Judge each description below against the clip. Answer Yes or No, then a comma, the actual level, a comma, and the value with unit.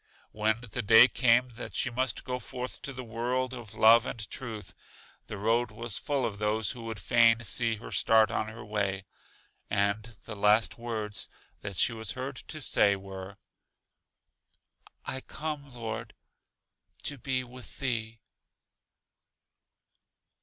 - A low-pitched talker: Yes, low, 115 Hz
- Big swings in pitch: No, average, 2.8 semitones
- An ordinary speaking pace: Yes, average, 145 wpm